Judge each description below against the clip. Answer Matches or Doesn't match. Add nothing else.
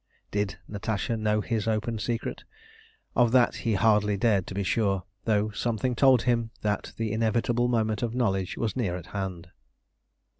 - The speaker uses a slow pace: Doesn't match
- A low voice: Matches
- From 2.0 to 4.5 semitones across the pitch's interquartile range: Matches